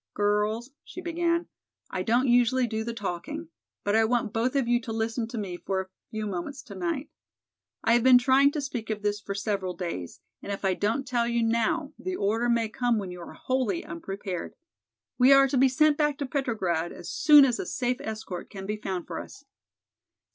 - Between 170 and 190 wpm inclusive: No, fast, 205 wpm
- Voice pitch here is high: Yes, high, 230 Hz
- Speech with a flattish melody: No, average, 4.4 semitones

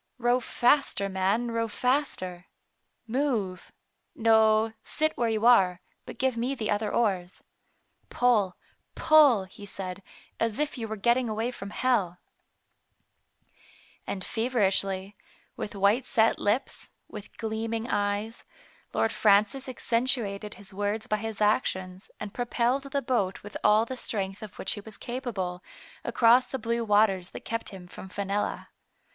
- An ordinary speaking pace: Yes, average, 145 wpm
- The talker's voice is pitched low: No, high, 220 Hz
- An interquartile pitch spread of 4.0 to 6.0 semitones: No, average, 3.3 semitones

